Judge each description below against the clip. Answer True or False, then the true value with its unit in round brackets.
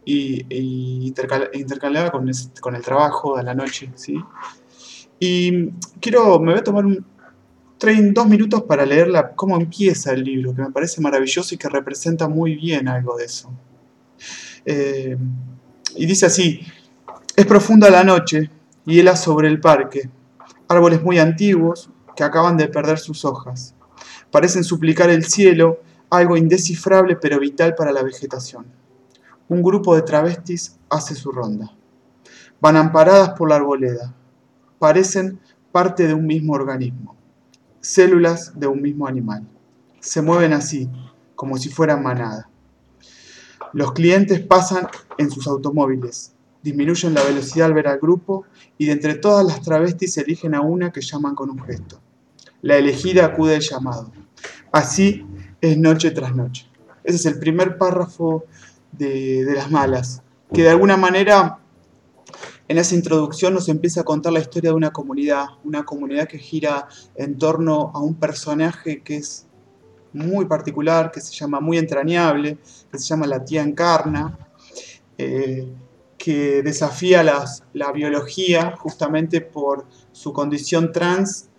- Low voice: False (155 Hz)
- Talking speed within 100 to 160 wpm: True (150 wpm)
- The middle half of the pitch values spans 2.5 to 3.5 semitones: False (3.9 semitones)